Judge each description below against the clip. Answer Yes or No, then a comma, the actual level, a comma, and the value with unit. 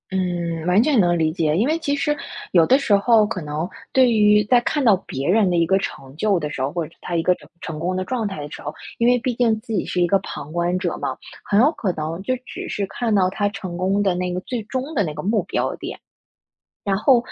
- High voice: Yes, high, 195 Hz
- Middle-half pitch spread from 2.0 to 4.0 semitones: No, average, 4.8 semitones